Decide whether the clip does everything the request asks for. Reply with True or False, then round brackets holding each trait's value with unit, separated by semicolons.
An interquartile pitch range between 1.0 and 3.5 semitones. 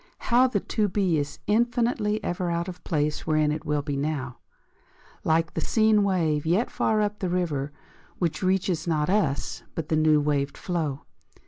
False (5.2 semitones)